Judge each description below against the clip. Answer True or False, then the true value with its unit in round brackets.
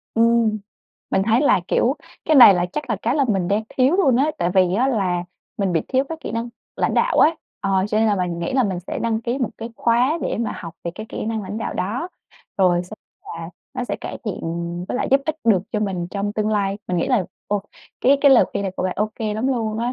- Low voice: False (215 Hz)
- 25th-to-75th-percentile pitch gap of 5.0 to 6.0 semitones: False (4.4 semitones)